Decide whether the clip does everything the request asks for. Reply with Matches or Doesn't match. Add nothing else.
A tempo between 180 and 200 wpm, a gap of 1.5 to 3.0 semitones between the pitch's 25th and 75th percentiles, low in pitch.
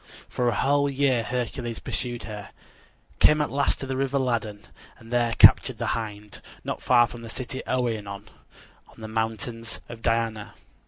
Doesn't match